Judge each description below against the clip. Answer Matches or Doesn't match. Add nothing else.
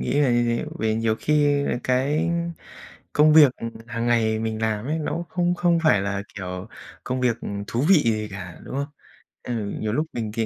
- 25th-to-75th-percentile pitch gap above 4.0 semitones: Matches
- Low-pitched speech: Matches